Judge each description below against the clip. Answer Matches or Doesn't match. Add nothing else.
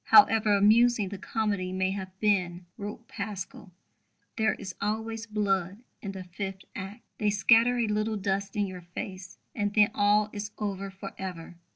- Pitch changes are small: Matches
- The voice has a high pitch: Matches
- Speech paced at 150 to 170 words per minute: Matches